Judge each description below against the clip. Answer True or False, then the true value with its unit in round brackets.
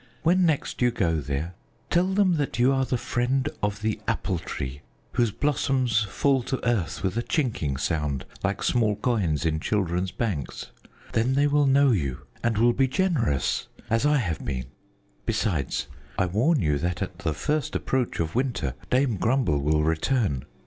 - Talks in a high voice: False (115 Hz)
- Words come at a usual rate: True (170 wpm)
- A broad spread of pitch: True (8.3 semitones)